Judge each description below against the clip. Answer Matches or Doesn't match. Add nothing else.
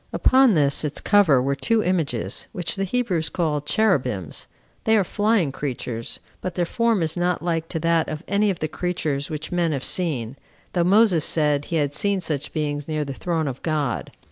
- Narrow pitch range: Doesn't match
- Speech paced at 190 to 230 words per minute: Matches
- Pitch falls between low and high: Matches